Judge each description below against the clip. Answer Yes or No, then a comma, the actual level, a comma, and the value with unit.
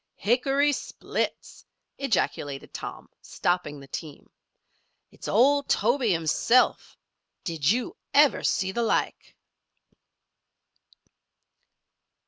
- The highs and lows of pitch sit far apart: Yes, wide, 8.1 semitones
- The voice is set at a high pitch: Yes, high, 220 Hz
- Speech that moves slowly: Yes, slow, 85 wpm